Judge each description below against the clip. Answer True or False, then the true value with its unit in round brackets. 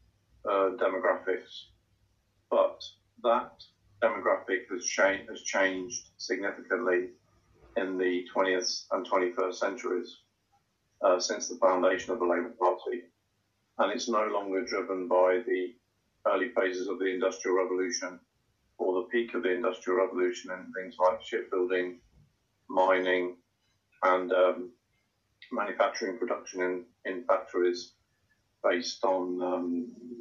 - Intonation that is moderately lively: False (1.8 semitones)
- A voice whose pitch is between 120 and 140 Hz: False (95 Hz)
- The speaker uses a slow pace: True (115 wpm)